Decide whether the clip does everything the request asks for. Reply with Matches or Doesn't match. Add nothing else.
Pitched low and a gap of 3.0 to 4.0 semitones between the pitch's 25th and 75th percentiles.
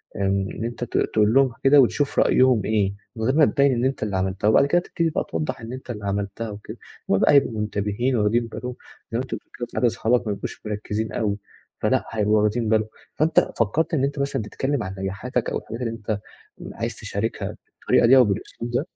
Matches